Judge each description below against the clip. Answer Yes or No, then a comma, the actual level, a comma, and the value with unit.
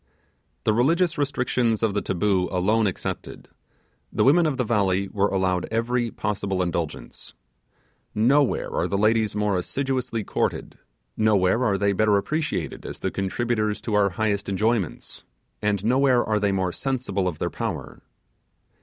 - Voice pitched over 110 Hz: No, low, 105 Hz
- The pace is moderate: Yes, average, 145 wpm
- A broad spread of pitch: No, average, 3.7 semitones